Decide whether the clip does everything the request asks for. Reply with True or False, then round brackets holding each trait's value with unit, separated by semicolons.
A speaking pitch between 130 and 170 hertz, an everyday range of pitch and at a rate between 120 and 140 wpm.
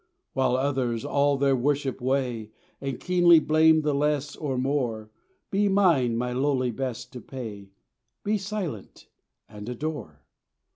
True (135 Hz; 3.6 semitones; 135 wpm)